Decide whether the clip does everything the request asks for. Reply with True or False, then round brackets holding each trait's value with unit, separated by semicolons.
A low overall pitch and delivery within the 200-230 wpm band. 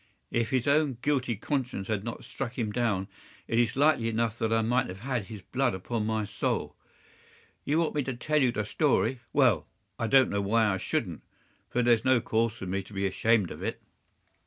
True (115 Hz; 205 wpm)